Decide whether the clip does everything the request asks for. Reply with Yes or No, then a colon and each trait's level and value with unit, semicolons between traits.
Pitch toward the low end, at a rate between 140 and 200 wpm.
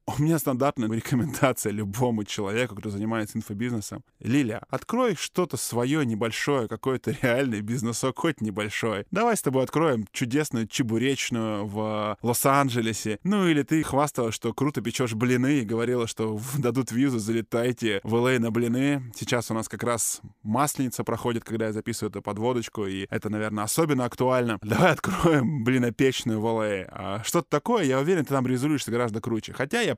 Yes: low, 120 Hz; average, 155 wpm